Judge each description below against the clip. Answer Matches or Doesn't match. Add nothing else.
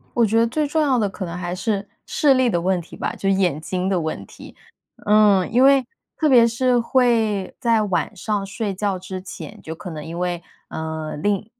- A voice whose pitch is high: Matches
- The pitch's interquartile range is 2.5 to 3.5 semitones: Doesn't match